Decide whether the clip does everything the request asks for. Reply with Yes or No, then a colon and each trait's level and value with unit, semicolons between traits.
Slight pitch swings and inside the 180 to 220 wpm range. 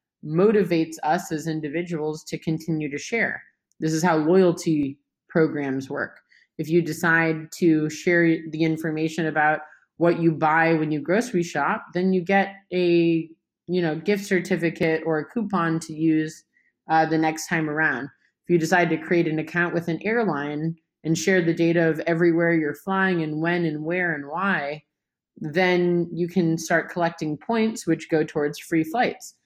No: narrow, 1.8 semitones; average, 165 wpm